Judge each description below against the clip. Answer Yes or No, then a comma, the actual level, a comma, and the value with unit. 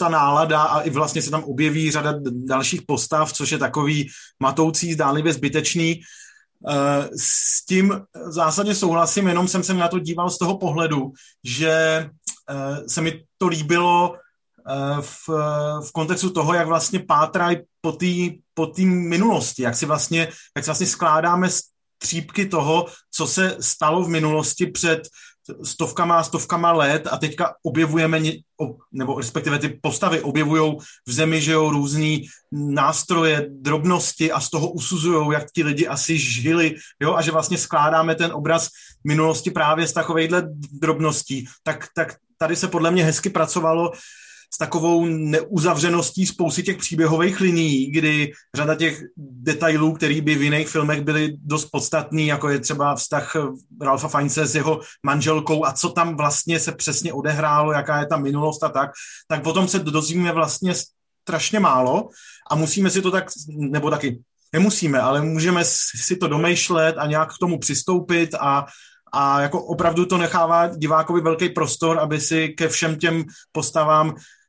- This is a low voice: No, medium, 160 Hz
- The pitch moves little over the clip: Yes, narrow, 2.2 semitones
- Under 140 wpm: No, average, 150 wpm